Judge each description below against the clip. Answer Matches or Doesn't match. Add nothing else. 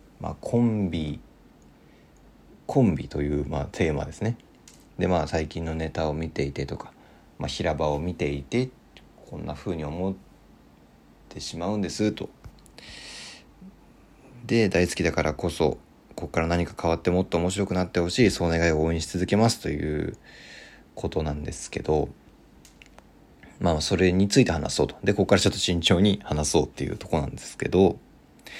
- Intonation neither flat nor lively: Matches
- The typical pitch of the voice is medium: Doesn't match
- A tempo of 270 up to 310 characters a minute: Doesn't match